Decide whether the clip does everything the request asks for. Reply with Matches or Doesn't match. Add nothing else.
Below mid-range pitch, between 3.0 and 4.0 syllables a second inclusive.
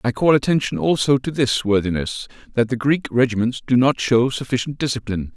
Doesn't match